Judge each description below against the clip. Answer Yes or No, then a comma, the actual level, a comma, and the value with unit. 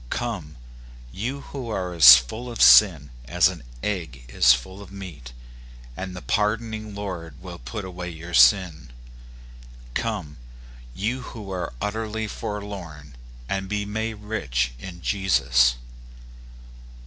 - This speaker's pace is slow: Yes, slow, 125 wpm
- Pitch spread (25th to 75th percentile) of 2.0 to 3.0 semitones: No, average, 5.3 semitones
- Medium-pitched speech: No, very low, 95 Hz